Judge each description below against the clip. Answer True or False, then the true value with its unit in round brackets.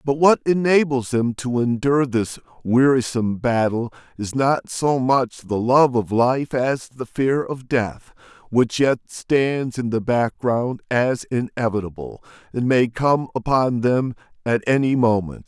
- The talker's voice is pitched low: True (125 Hz)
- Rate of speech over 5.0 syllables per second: False (4.0 syllables/s)